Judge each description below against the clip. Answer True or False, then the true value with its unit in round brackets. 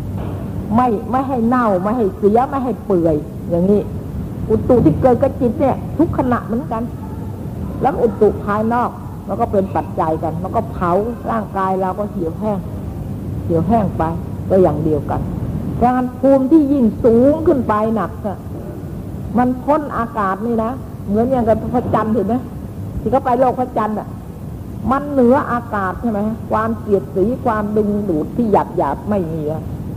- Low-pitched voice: False (220 Hz)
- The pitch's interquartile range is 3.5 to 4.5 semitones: True (4.1 semitones)